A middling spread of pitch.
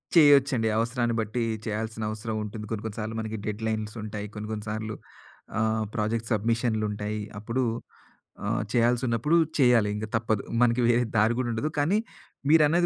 No: narrow, 2.2 semitones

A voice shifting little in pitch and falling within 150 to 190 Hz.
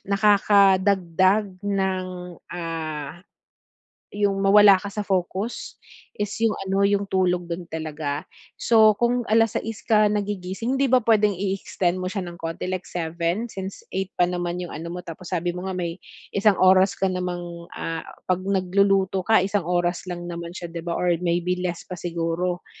Yes: narrow, 2.3 semitones; medium, 185 Hz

